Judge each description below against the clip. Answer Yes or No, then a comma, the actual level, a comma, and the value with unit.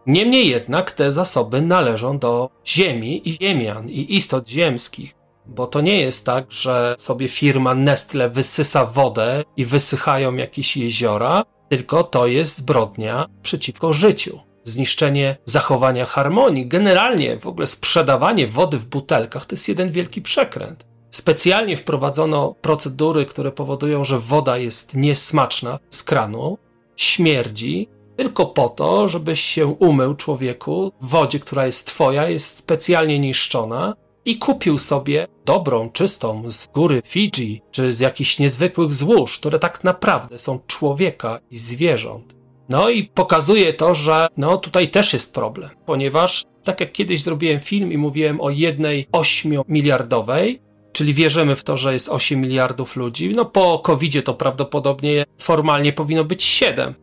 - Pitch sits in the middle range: Yes, medium, 145 Hz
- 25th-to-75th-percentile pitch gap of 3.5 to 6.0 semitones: Yes, average, 4.3 semitones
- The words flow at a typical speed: Yes, average, 140 wpm